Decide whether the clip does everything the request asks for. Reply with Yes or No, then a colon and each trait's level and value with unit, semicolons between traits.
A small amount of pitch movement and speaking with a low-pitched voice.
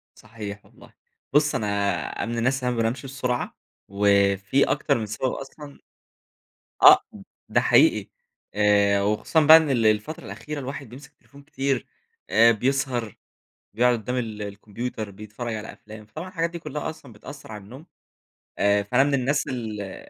No: average, 4.6 semitones; low, 115 Hz